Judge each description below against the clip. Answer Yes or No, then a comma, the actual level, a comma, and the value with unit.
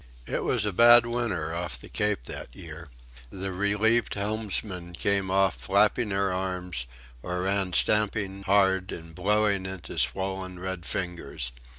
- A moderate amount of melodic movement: No, narrow, 2.3 semitones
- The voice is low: Yes, very low, 95 Hz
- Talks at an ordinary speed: Yes, average, 145 wpm